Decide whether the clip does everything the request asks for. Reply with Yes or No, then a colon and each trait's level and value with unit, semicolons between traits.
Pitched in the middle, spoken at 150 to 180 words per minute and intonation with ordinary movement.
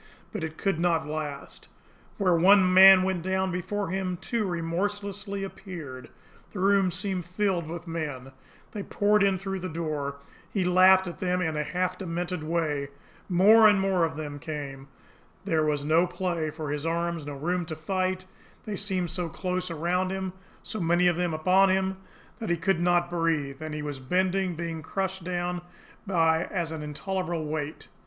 Yes: medium, 175 Hz; average, 175 wpm; average, 3.0 semitones